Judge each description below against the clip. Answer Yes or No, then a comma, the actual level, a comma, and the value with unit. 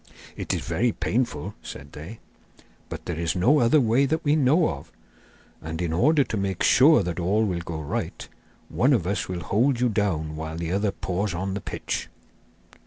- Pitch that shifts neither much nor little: No, wide, 6.6 semitones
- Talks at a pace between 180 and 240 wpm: Yes, average, 190 wpm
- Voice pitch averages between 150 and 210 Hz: No, low, 100 Hz